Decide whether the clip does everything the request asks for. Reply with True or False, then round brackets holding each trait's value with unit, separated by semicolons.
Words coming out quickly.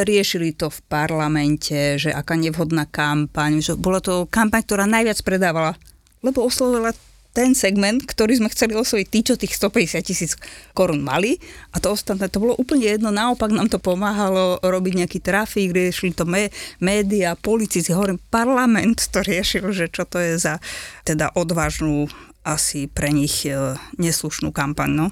False (155 wpm)